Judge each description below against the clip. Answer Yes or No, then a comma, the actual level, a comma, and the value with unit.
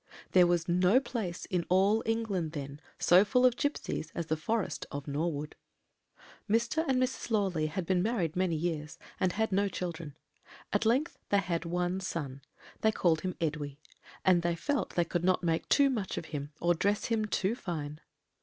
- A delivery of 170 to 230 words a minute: Yes, average, 180 wpm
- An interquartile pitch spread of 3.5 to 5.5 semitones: Yes, average, 4.7 semitones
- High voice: No, medium, 180 Hz